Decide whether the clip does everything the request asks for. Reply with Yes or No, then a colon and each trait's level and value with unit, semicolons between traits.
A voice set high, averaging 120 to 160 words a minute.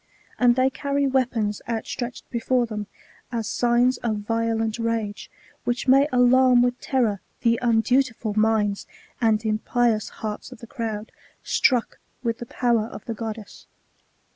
Yes: high, 230 Hz; average, 140 wpm